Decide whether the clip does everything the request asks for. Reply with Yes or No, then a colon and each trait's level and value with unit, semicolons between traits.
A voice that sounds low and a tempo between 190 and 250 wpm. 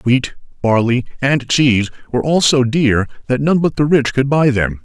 Yes: low, 130 Hz; average, 200 wpm